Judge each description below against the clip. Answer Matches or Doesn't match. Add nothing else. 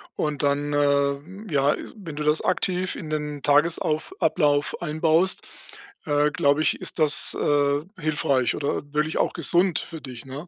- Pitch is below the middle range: Doesn't match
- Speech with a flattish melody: Matches